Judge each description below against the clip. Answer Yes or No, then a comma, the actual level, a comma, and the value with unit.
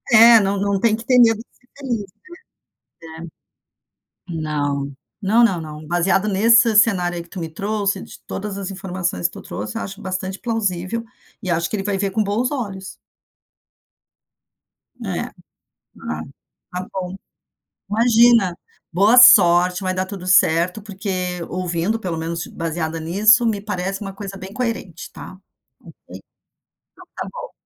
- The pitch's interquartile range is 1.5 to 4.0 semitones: Yes, average, 3.7 semitones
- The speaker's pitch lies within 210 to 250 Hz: No, high, 195 Hz